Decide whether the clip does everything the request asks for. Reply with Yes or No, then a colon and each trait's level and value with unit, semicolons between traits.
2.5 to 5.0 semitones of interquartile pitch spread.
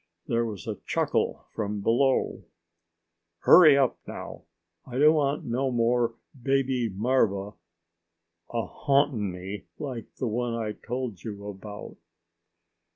Yes: average, 4.1 semitones